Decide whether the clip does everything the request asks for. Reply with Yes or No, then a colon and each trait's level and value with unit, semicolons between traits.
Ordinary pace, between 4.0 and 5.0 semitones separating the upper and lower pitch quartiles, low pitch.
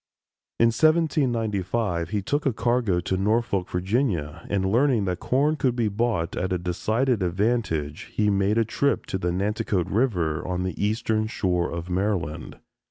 Yes: average, 160 wpm; average, 4.6 semitones; low, 105 Hz